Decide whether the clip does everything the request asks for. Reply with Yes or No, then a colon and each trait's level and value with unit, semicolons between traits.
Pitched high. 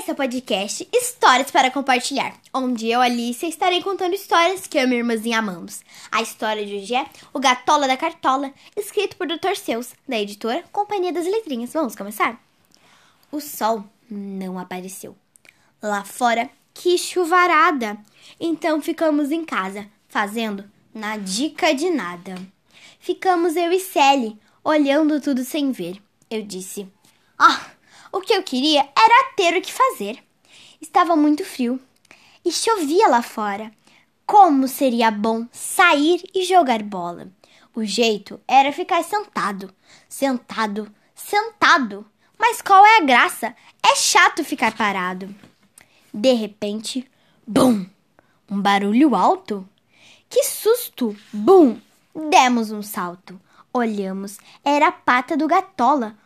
Yes: very high, 260 Hz